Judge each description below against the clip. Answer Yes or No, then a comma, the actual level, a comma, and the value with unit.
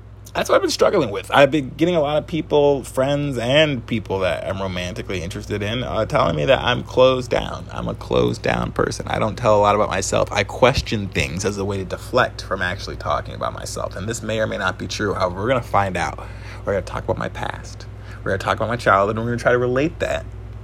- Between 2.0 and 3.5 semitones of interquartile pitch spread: No, average, 4.1 semitones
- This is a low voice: Yes, low, 105 Hz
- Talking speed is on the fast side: Yes, fast, 260 wpm